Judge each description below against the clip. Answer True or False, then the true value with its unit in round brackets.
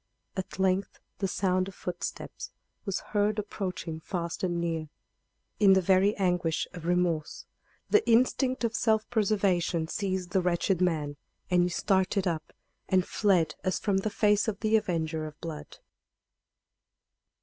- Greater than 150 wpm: False (145 wpm)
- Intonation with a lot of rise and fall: False (3.0 semitones)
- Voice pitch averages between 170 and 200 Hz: True (185 Hz)